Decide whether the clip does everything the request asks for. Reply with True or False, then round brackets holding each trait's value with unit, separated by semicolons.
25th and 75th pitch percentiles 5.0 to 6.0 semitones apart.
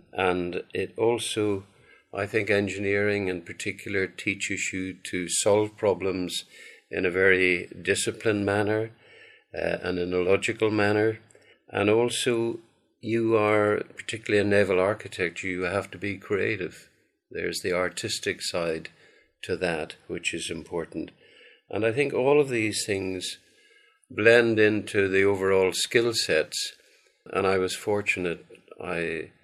False (3.1 semitones)